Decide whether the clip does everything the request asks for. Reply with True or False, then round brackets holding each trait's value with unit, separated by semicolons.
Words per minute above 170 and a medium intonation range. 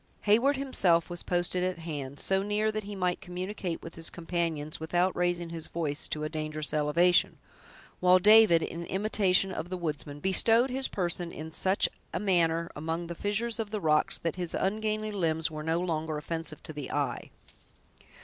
True (180 wpm; 3.4 semitones)